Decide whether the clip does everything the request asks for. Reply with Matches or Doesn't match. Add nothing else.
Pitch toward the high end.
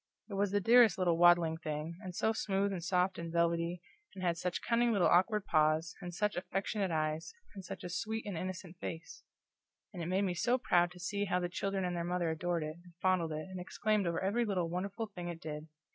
Doesn't match